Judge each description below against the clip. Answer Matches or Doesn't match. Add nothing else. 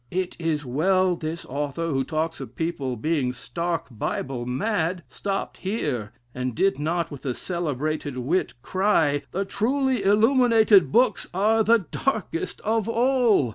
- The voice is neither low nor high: Matches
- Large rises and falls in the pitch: Matches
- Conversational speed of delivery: Matches